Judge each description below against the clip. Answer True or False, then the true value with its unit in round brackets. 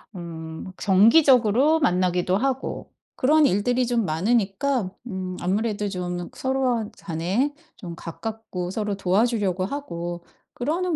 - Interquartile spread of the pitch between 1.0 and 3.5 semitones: False (5.5 semitones)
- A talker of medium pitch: False (205 Hz)